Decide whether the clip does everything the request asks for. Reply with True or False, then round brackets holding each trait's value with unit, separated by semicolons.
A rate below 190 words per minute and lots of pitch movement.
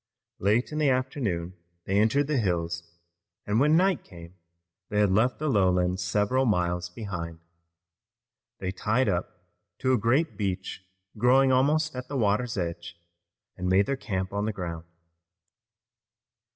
True (145 wpm; 6.2 semitones)